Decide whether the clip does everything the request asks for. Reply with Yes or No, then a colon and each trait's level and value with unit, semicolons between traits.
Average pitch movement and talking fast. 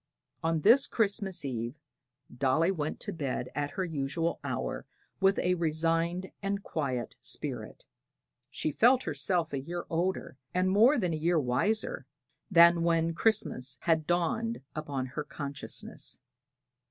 No: average, 4.6 semitones; average, 140 wpm